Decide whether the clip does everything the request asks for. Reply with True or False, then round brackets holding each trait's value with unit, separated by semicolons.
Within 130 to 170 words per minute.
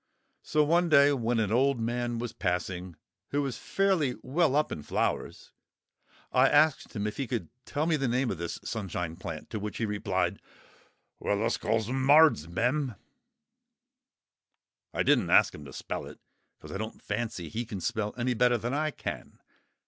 True (165 wpm)